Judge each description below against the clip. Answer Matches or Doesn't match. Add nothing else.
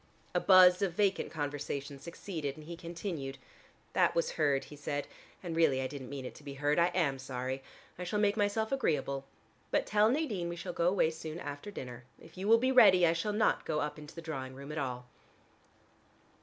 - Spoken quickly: Matches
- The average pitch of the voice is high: Doesn't match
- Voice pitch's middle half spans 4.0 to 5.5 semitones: Matches